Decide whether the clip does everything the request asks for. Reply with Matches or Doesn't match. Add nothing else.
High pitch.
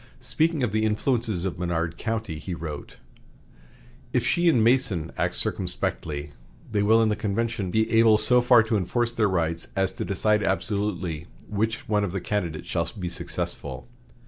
Doesn't match